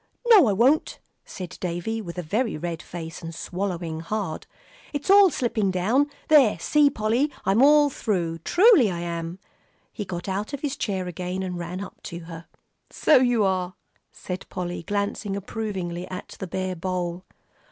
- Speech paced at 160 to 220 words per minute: Yes, average, 165 wpm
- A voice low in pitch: No, high, 190 Hz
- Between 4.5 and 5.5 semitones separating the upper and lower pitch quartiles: Yes, average, 4.8 semitones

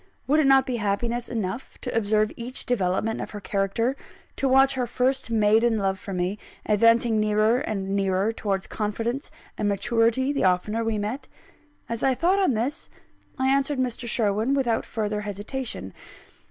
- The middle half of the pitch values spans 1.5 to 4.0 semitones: Yes, average, 3.6 semitones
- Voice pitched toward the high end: Yes, high, 225 Hz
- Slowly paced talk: No, average, 165 wpm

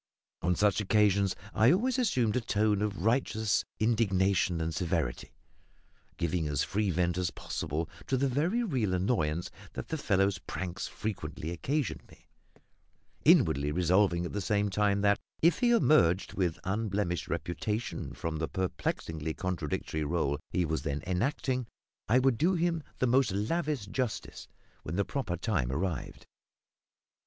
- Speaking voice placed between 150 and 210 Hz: No, low, 100 Hz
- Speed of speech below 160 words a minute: Yes, average, 145 wpm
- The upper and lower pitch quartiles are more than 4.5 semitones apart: Yes, wide, 5.4 semitones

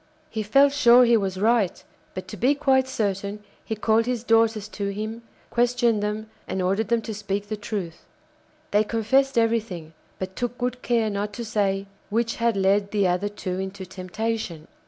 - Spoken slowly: No, average, 175 wpm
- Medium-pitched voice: No, high, 215 Hz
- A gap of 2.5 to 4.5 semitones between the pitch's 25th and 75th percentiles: Yes, average, 2.8 semitones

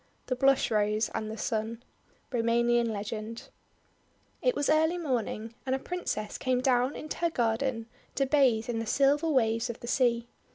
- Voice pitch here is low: No, high, 240 Hz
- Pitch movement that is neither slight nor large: Yes, average, 3.4 semitones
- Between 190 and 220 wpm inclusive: No, average, 165 wpm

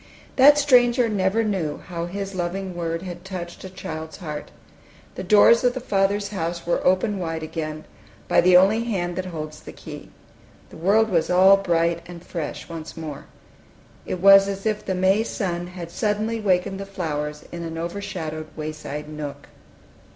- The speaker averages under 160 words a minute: No, average, 170 wpm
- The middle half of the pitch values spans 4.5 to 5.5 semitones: No, average, 3.3 semitones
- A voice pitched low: No, medium, 180 Hz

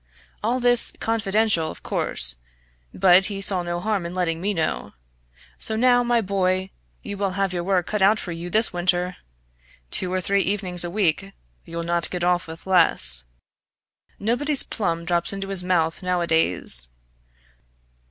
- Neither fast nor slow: Yes, average, 160 wpm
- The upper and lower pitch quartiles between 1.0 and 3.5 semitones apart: Yes, average, 2.8 semitones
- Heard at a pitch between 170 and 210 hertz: Yes, medium, 185 Hz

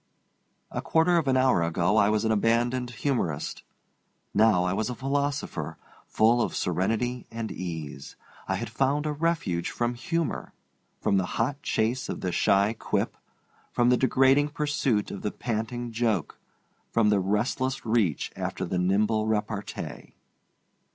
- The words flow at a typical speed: Yes, average, 150 wpm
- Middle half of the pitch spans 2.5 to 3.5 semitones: No, average, 4.5 semitones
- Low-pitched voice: Yes, low, 115 Hz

